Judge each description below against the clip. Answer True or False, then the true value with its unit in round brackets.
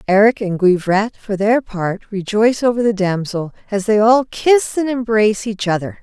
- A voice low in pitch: False (210 Hz)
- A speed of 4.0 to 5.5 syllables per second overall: True (4.8 syllables/s)